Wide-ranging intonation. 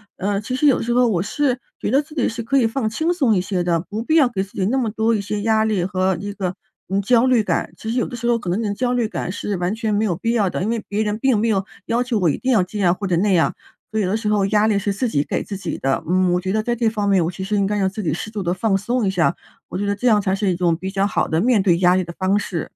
No: average, 3.4 semitones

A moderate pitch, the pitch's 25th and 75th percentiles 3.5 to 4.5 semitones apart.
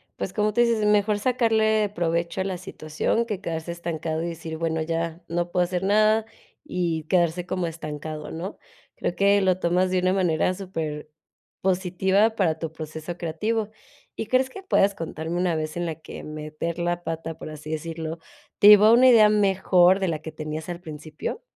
Yes: medium, 175 Hz; average, 3.8 semitones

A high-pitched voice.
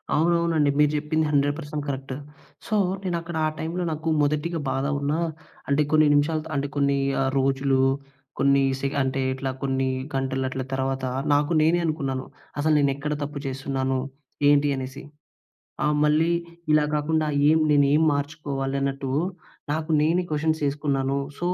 No: medium, 145 Hz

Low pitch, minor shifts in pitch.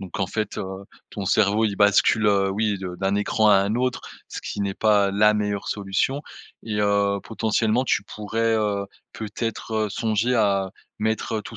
Yes: low, 105 Hz; narrow, 1.9 semitones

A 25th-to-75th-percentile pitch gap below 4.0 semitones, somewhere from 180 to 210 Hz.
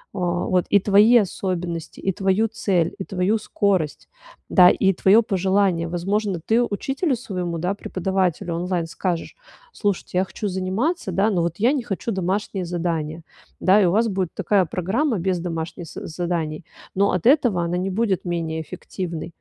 Yes: average, 2.9 semitones; medium, 185 Hz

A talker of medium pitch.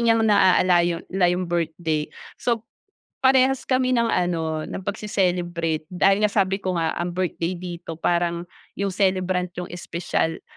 Yes: medium, 180 Hz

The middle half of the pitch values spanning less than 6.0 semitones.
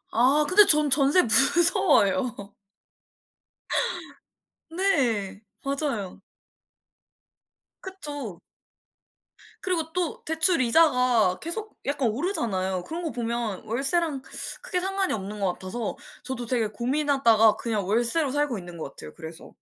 No: wide, 6.8 semitones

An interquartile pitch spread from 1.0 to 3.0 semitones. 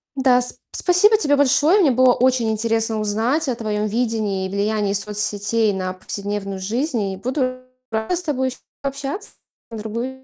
No: average, 4.0 semitones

